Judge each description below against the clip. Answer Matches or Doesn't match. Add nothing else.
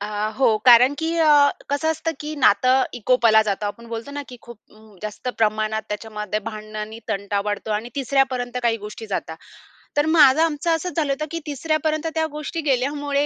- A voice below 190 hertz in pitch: Doesn't match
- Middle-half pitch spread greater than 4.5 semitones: Matches